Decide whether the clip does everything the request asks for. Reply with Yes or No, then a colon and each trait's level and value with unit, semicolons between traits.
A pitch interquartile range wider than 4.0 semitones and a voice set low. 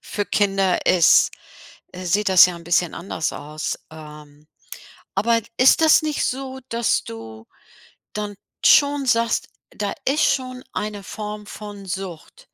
No: wide, 5.5 semitones; high, 205 Hz